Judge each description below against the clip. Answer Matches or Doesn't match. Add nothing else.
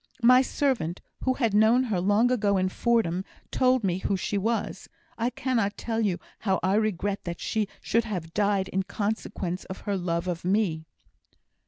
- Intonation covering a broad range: Doesn't match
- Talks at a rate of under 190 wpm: Matches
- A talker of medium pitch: Doesn't match